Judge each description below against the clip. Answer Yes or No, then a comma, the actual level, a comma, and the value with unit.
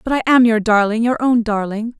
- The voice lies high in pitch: Yes, high, 230 Hz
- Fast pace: Yes, fast, 240 wpm